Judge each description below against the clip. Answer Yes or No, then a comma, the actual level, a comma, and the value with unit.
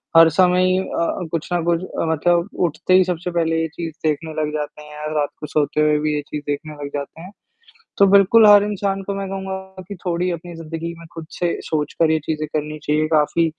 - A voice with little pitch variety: No, average, 3.1 semitones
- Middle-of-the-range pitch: Yes, medium, 165 Hz